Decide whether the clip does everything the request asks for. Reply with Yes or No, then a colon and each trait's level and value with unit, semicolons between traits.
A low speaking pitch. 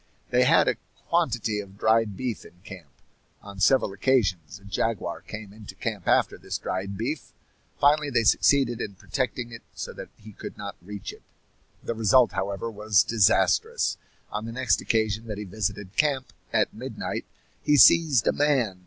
Yes: low, 110 Hz